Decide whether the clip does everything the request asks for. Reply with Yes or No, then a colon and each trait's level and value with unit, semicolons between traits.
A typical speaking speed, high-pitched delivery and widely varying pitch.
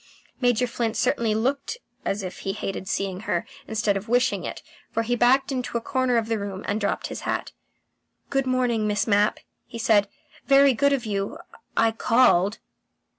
No: average, 180 wpm; high, 225 Hz; average, 3.4 semitones